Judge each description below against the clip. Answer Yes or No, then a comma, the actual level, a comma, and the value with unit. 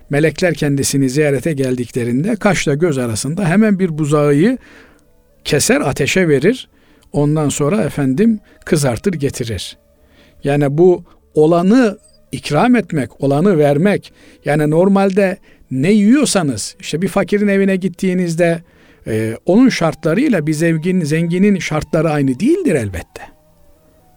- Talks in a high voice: No, medium, 160 Hz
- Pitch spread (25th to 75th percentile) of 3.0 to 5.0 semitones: No, wide, 5.5 semitones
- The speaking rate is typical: Yes, average, 105 wpm